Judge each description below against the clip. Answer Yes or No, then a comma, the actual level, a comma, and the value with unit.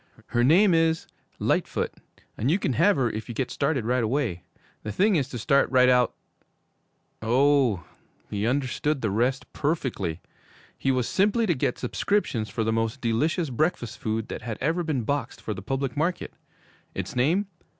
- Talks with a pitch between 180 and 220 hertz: No, low, 130 Hz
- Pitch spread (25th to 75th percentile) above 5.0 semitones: Yes, wide, 5.4 semitones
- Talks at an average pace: Yes, average, 175 wpm